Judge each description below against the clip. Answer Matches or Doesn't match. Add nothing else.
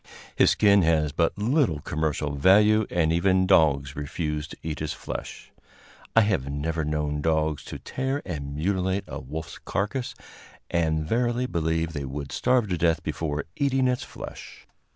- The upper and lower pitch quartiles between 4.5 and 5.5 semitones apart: Matches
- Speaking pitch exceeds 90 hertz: Doesn't match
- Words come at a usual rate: Matches